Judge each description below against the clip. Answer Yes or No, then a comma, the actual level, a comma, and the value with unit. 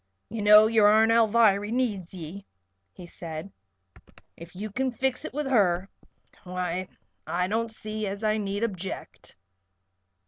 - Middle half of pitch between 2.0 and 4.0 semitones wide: Yes, average, 3.4 semitones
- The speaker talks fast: No, average, 140 wpm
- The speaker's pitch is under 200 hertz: No, high, 205 Hz